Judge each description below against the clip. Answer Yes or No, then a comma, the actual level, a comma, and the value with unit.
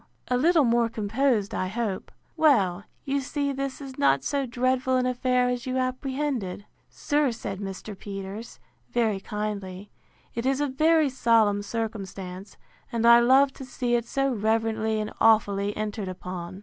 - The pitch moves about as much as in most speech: Yes, average, 4.3 semitones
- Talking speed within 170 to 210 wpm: No, average, 155 wpm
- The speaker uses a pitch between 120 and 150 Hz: No, high, 230 Hz